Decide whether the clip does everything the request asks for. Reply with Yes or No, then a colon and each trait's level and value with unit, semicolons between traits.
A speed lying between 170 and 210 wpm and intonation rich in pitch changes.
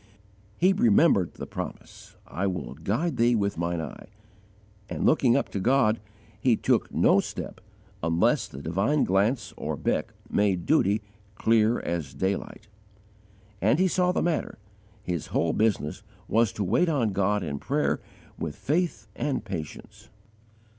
No: average, 145 wpm; wide, 7.1 semitones